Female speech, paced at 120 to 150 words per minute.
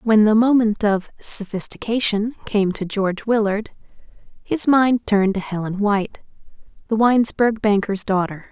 Yes: female; slow, 135 wpm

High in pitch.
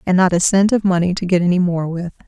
No: medium, 180 Hz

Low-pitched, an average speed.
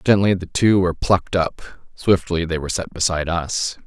Yes: very low, 90 Hz; average, 185 wpm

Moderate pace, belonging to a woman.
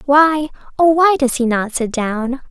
Yes: average, 190 wpm; female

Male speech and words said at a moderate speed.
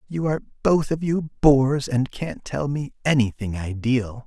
Yes: male; average, 170 wpm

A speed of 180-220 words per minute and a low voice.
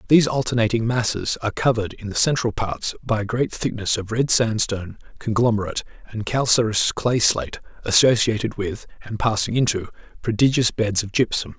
No: average, 155 wpm; low, 110 Hz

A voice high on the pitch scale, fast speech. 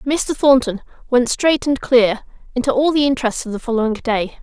No: very high, 255 Hz; average, 190 wpm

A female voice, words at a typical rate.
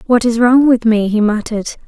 No: female; fast, 225 wpm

